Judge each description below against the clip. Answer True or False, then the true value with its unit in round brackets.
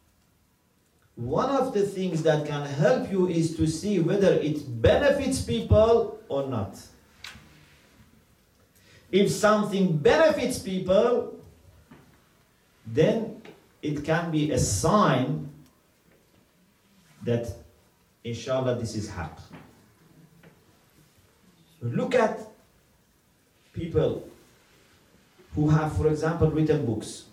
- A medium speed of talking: False (90 wpm)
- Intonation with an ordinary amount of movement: False (8.6 semitones)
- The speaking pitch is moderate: True (155 Hz)